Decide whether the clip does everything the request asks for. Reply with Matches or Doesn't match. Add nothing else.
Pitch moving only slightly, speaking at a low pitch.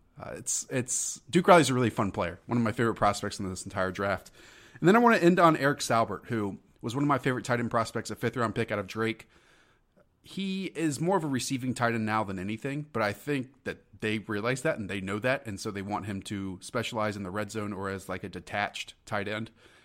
Doesn't match